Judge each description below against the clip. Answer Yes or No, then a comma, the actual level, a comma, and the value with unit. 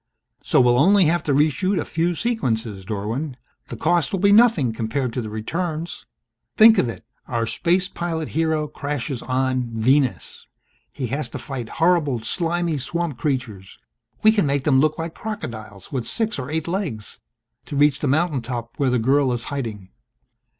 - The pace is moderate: Yes, average, 170 wpm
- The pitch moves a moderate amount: No, wide, 5.8 semitones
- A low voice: No, medium, 145 Hz